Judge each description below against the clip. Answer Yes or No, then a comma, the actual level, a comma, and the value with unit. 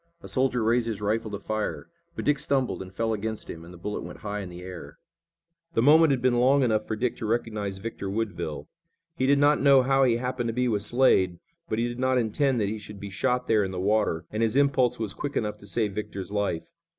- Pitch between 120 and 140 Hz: No, low, 110 Hz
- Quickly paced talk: Yes, fast, 245 wpm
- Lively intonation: No, average, 3.8 semitones